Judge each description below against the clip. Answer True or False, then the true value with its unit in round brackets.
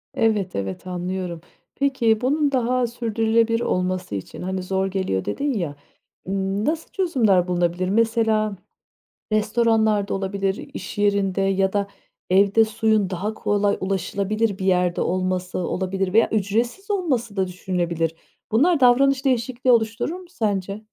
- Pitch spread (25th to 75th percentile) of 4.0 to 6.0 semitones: False (3.6 semitones)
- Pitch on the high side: True (205 Hz)